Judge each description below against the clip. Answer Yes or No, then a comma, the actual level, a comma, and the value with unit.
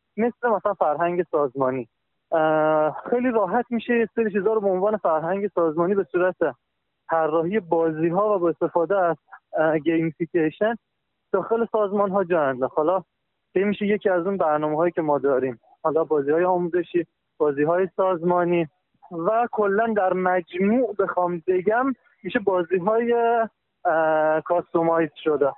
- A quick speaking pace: No, average, 130 wpm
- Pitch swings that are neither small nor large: Yes, average, 4.1 semitones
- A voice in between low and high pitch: Yes, medium, 180 Hz